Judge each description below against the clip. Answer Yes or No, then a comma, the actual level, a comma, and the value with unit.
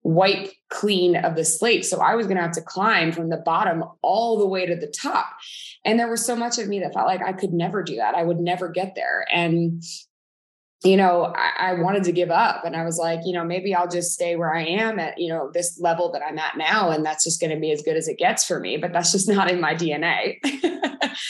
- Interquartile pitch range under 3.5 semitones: Yes, average, 3.1 semitones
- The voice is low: No, medium, 180 Hz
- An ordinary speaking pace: No, fast, 260 wpm